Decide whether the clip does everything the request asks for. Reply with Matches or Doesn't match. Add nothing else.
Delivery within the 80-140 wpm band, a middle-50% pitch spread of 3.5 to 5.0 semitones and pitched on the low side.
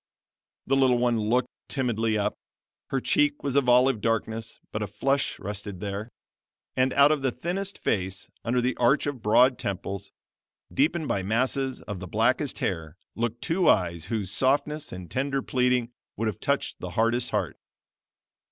Doesn't match